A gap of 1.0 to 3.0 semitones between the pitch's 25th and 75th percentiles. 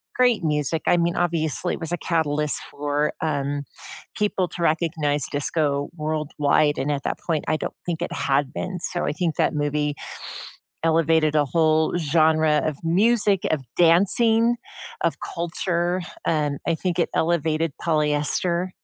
Yes: narrow, 2.6 semitones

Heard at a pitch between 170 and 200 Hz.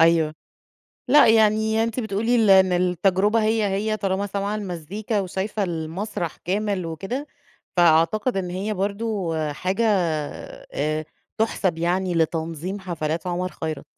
Yes: high, 190 Hz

